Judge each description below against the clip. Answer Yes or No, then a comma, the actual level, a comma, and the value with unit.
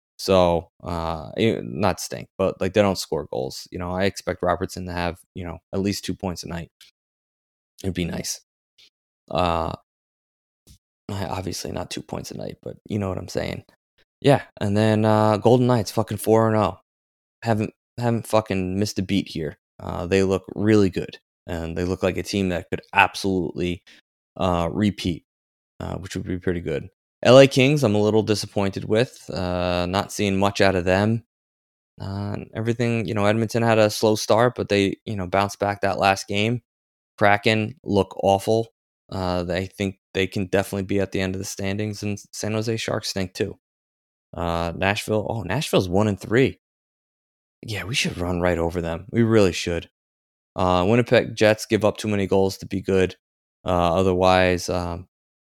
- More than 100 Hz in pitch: No, very low, 95 Hz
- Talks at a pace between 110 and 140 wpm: No, average, 175 wpm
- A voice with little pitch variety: No, average, 3.2 semitones